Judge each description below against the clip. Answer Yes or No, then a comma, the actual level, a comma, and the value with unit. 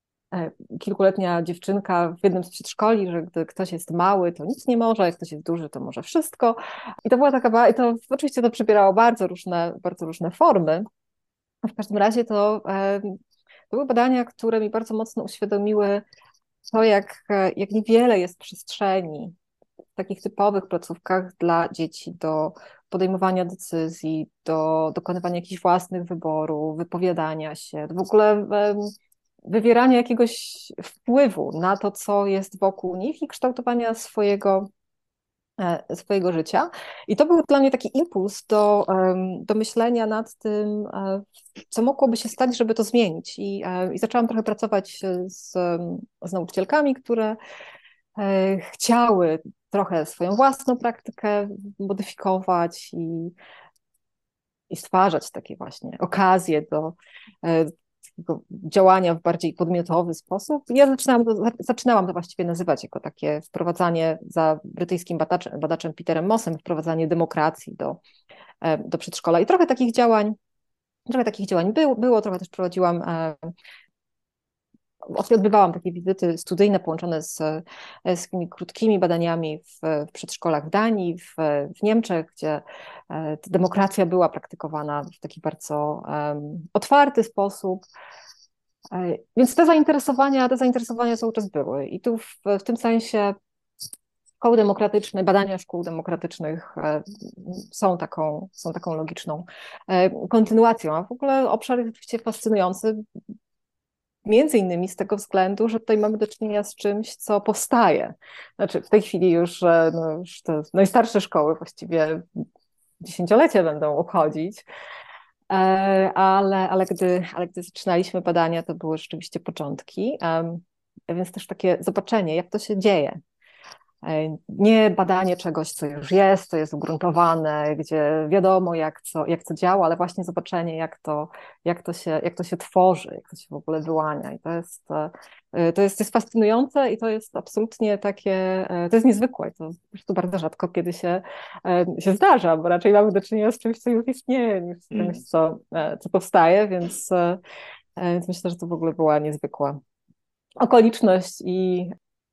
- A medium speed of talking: Yes, average, 145 wpm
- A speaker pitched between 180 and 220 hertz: Yes, high, 190 Hz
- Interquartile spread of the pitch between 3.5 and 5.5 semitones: Yes, average, 4.3 semitones